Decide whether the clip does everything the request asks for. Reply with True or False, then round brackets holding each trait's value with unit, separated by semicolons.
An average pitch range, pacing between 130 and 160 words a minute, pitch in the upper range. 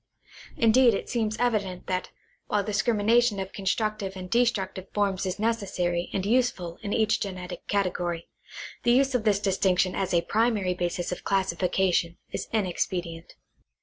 True (3.2 semitones; 150 wpm; 195 Hz)